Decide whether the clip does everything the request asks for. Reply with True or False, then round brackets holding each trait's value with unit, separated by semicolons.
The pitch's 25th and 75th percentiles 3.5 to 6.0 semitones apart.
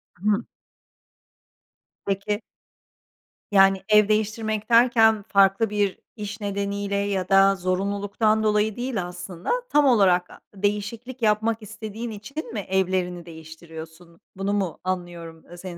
False (2.6 semitones)